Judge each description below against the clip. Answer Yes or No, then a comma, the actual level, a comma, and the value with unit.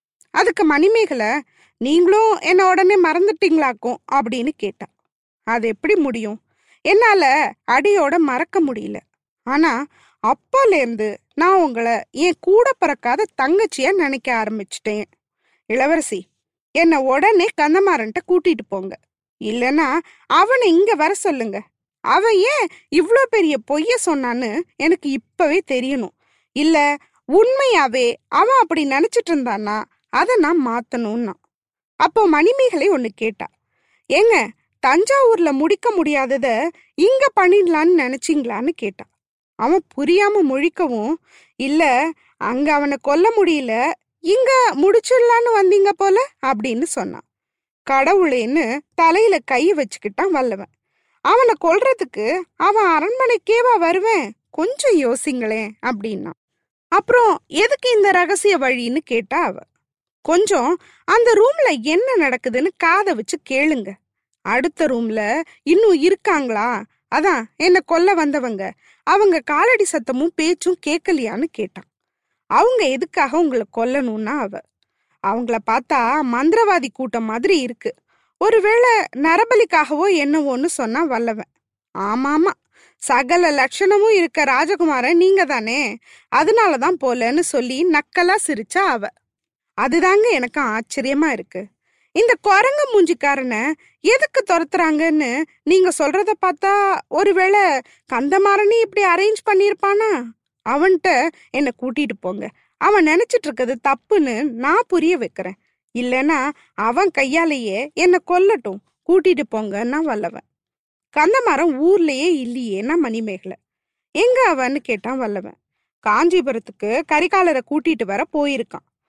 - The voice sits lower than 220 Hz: No, very high, 325 Hz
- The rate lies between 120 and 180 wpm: No, average, 100 wpm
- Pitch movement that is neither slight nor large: No, wide, 7.0 semitones